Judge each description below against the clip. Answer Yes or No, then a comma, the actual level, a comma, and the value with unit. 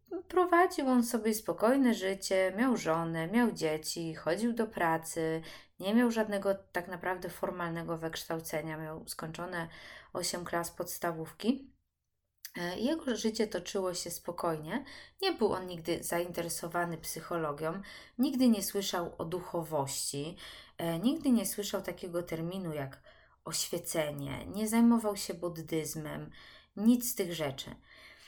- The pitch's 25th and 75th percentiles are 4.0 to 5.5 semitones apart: Yes, average, 5.1 semitones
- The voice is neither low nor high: Yes, medium, 175 Hz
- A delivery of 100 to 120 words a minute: Yes, average, 115 wpm